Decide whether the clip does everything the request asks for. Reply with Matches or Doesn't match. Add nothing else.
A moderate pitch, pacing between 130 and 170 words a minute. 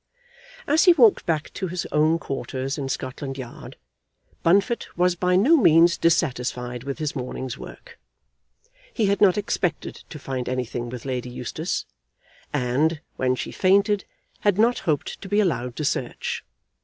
Matches